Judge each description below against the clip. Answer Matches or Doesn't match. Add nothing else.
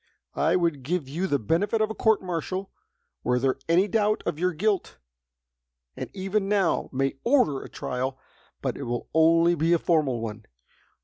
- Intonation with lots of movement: Matches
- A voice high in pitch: Doesn't match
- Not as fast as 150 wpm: Doesn't match